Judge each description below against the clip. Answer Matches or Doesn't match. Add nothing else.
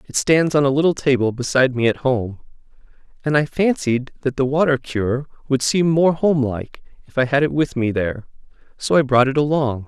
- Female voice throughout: Doesn't match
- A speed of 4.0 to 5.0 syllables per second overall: Doesn't match